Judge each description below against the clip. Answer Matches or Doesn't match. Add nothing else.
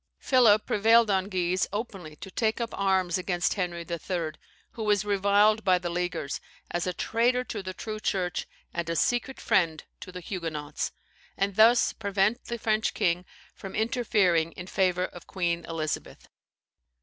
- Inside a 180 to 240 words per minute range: Doesn't match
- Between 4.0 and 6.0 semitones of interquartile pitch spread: Doesn't match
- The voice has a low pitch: Doesn't match